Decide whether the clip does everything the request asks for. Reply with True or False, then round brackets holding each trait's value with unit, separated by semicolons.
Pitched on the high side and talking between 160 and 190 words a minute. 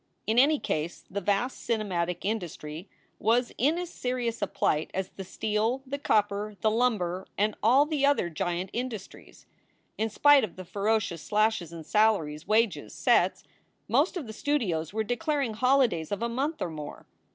True (215 Hz; 165 wpm)